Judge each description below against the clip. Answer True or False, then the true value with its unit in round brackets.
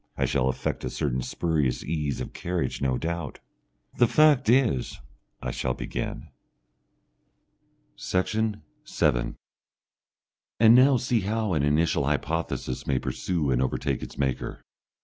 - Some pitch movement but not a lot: False (8.8 semitones)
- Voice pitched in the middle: False (80 Hz)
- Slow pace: True (130 wpm)